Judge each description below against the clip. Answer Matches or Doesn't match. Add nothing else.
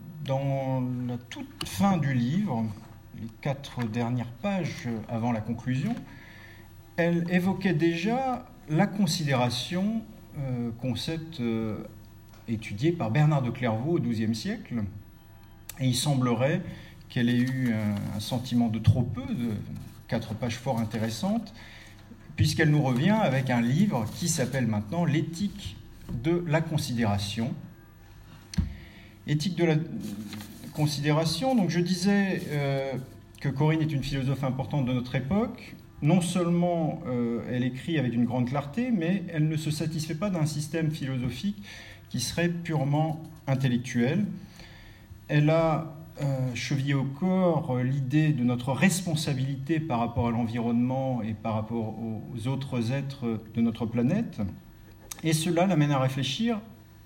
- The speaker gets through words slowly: Matches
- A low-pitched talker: Matches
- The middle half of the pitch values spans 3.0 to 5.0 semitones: Doesn't match